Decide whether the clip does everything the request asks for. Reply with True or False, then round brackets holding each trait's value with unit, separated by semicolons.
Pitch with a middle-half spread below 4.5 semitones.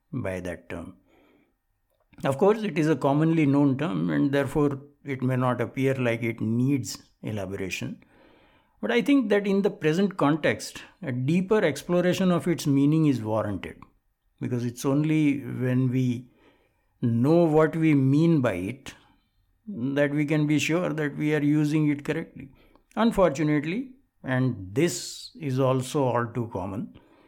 True (4.1 semitones)